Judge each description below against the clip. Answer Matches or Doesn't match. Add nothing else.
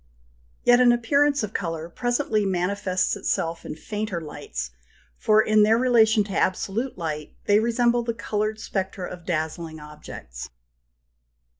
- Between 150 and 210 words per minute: Doesn't match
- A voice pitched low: Doesn't match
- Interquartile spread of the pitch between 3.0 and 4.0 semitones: Doesn't match